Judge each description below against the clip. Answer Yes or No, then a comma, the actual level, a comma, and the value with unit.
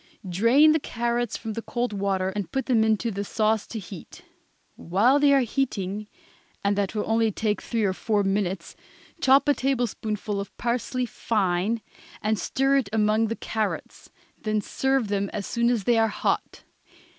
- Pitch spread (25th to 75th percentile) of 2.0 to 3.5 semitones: Yes, average, 3.1 semitones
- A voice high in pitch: Yes, high, 220 Hz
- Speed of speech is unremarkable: Yes, average, 170 wpm